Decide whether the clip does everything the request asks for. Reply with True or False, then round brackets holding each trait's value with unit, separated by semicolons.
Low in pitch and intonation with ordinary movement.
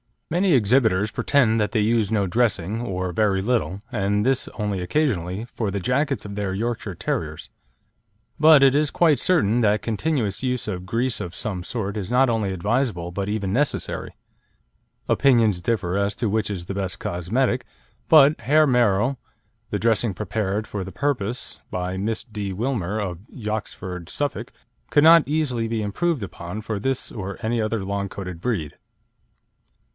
True (110 Hz; 4.4 semitones)